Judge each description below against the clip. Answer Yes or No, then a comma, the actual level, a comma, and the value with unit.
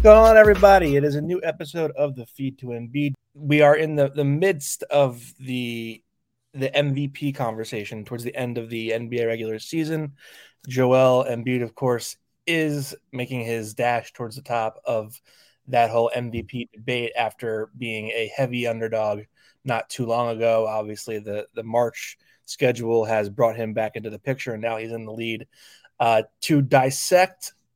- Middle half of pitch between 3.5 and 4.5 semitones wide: Yes, average, 3.8 semitones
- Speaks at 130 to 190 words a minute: Yes, average, 170 wpm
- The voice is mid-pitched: No, low, 120 Hz